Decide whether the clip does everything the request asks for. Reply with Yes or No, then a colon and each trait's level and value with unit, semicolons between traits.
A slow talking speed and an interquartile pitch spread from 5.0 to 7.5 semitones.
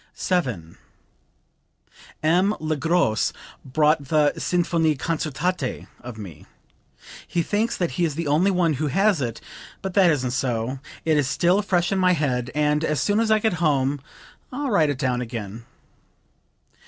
No: average, 155 wpm; wide, 5.4 semitones